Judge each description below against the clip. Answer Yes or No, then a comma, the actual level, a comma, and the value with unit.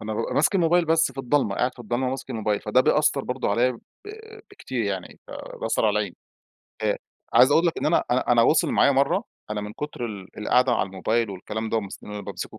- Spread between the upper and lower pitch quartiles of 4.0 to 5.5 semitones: Yes, average, 4.4 semitones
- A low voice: Yes, low, 120 Hz